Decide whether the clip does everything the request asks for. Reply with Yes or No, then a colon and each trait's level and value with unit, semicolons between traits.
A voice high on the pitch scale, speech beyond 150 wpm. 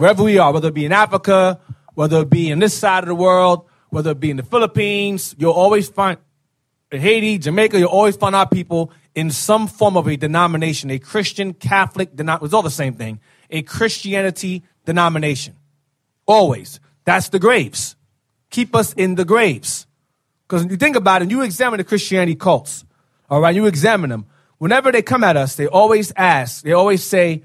No: medium, 175 Hz; average, 190 wpm